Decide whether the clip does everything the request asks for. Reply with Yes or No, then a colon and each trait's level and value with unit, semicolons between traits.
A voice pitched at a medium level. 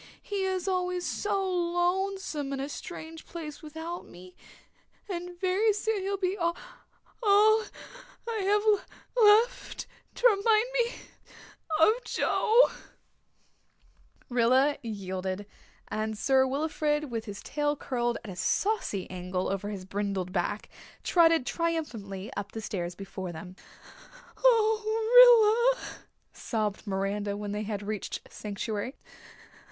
No: very high, 300 Hz